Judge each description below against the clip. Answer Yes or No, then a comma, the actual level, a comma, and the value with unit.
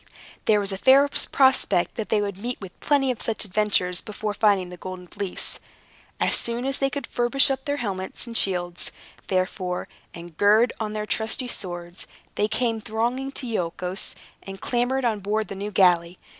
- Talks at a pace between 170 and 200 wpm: Yes, average, 180 wpm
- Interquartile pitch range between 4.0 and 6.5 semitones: Yes, average, 4.5 semitones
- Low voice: No, high, 210 Hz